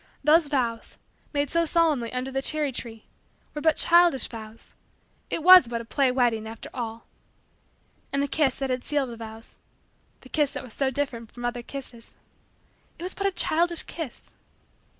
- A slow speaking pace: No, average, 175 wpm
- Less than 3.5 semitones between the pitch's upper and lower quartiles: No, average, 4.7 semitones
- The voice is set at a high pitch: Yes, very high, 265 Hz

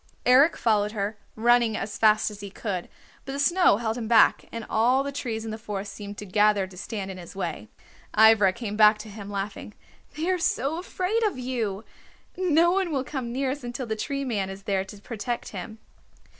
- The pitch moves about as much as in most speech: Yes, average, 4.3 semitones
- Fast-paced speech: Yes, fast, 210 wpm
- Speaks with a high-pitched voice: Yes, high, 220 Hz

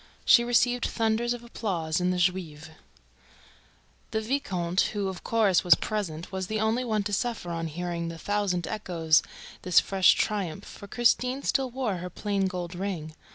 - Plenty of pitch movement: No, average, 4.1 semitones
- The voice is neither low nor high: No, high, 195 Hz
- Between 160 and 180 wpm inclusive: Yes, average, 170 wpm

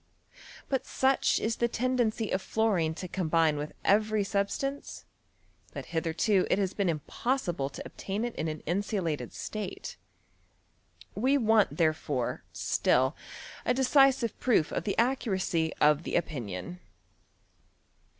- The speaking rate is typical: No, slow, 130 wpm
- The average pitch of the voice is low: No, high, 195 Hz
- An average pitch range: No, wide, 6.3 semitones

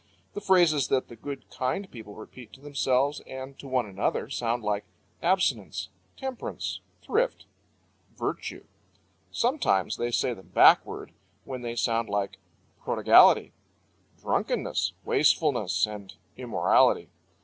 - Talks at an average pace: No, slow, 115 wpm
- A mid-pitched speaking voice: No, low, 130 Hz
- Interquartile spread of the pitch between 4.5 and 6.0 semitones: Yes, average, 5.1 semitones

